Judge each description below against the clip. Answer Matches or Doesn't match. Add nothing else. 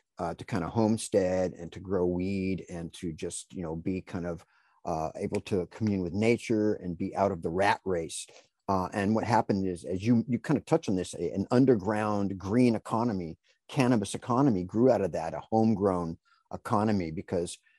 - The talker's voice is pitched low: Matches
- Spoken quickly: Doesn't match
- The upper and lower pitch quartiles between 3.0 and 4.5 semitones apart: Matches